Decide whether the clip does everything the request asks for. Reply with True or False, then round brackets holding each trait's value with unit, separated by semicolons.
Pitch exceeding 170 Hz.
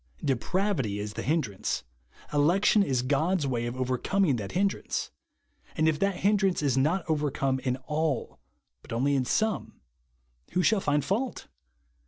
False (150 Hz)